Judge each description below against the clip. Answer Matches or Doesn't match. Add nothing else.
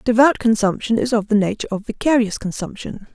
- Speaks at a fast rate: Doesn't match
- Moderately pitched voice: Doesn't match